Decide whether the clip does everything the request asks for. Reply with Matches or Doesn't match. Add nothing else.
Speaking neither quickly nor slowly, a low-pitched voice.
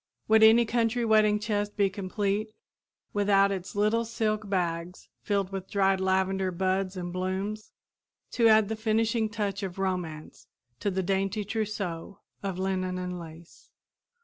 Doesn't match